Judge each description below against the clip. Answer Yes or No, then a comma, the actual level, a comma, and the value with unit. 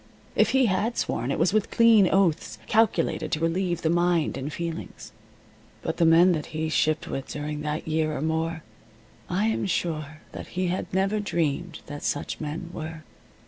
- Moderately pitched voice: Yes, medium, 165 Hz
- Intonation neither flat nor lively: Yes, average, 3.1 semitones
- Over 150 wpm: Yes, average, 180 wpm